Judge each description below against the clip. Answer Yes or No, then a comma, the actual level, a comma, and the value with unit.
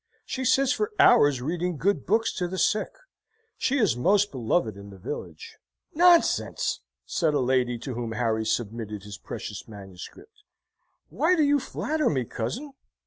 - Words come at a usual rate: Yes, average, 155 wpm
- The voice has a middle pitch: Yes, medium, 145 Hz